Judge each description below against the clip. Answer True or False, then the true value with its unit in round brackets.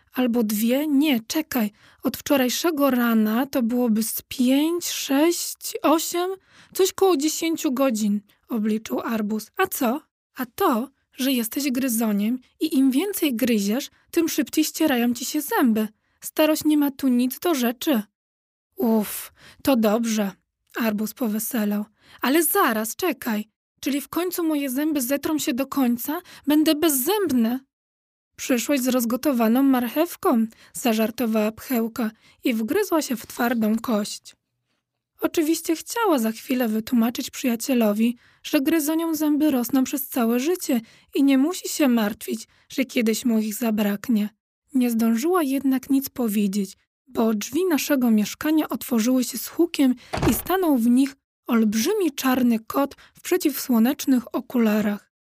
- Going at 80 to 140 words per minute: True (130 wpm)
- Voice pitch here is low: False (260 Hz)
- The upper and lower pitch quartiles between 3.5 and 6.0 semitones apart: True (5.2 semitones)